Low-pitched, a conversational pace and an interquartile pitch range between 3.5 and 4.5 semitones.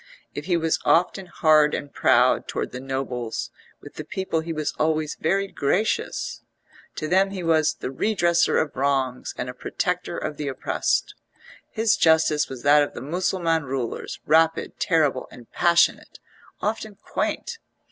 No: medium, 155 Hz; average, 155 wpm; average, 4.2 semitones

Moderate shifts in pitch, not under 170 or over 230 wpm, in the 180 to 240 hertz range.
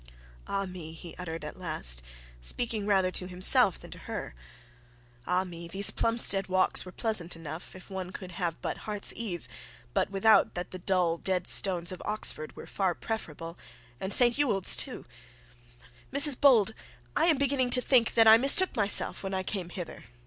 Yes: average, 4.0 semitones; average, 175 wpm; high, 190 Hz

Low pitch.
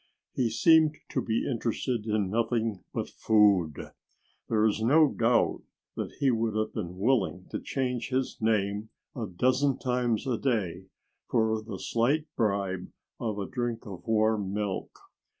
Yes: low, 110 Hz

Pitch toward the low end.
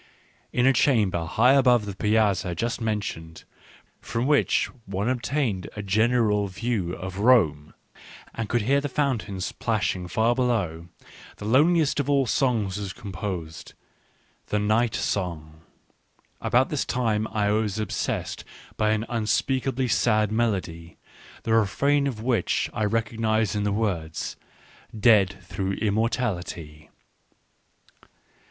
Yes: low, 110 Hz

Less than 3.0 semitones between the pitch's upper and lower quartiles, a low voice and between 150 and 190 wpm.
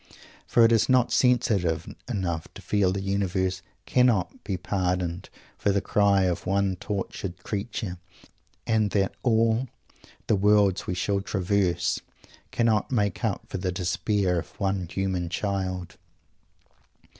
No: narrow, 2.4 semitones; low, 100 Hz; slow, 135 wpm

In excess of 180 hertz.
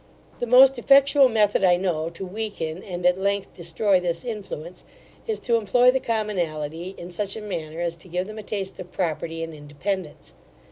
Yes: high, 190 Hz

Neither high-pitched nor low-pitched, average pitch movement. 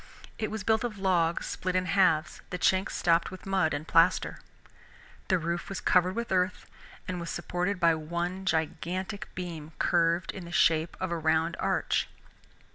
No: medium, 180 Hz; narrow, 2.1 semitones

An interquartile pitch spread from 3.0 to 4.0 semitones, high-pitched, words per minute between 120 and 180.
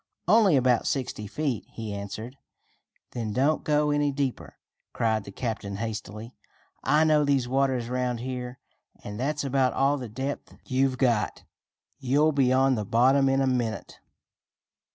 No: average, 3.3 semitones; low, 130 Hz; average, 150 wpm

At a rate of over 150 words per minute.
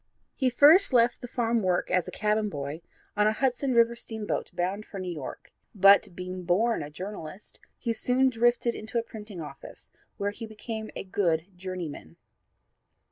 Yes: average, 170 wpm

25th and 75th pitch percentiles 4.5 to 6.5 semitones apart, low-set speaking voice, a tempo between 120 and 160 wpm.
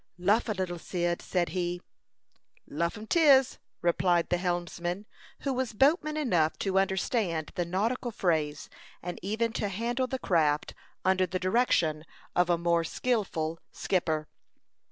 No: average, 4.8 semitones; medium, 185 Hz; average, 140 wpm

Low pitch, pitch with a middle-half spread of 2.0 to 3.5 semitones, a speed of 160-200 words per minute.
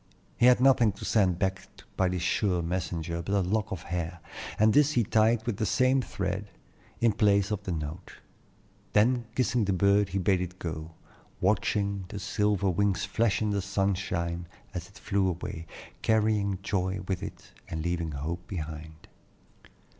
Yes: very low, 95 Hz; average, 3.2 semitones; average, 170 wpm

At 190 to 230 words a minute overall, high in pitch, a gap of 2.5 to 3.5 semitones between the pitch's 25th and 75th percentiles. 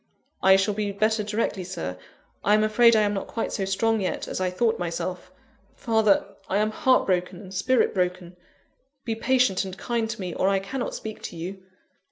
Yes: average, 200 wpm; high, 200 Hz; average, 3.0 semitones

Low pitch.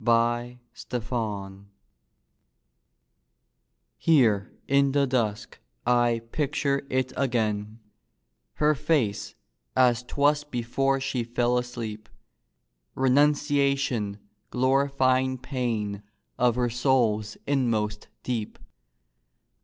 Yes: low, 125 Hz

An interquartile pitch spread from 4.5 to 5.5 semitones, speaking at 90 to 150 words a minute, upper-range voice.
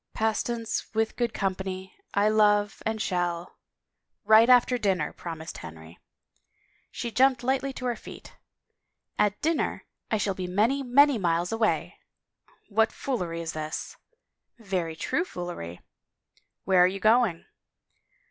Yes: average, 5.0 semitones; average, 140 wpm; high, 205 Hz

